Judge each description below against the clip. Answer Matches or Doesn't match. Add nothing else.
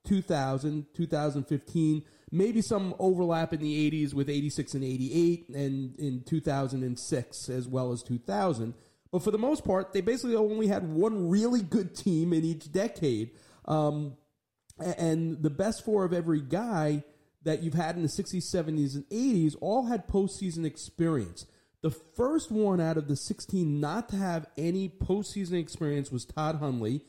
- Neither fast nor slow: Matches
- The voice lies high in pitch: Doesn't match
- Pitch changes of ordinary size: Matches